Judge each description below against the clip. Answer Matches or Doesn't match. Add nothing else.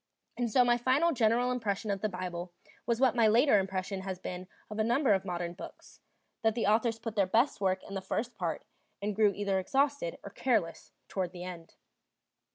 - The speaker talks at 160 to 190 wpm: Doesn't match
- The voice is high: Matches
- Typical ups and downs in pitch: Matches